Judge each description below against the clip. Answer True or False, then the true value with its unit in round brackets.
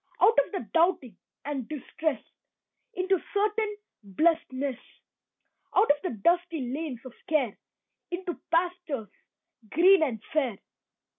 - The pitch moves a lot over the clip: True (5.7 semitones)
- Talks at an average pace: False (115 wpm)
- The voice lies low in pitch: False (315 Hz)